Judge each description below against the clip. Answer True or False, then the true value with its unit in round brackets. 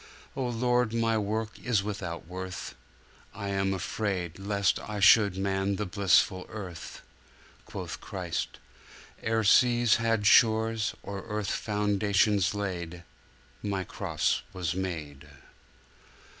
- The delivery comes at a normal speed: False (115 wpm)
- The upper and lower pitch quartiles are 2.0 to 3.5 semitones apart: True (2.7 semitones)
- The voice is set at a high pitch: False (100 Hz)